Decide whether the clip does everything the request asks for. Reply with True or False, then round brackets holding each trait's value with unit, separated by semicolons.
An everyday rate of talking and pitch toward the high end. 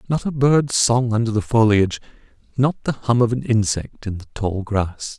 False (195 wpm; 115 Hz)